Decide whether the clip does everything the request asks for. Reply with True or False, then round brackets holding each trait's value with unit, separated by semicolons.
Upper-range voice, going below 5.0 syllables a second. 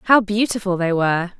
False (195 Hz; 5.4 syllables/s)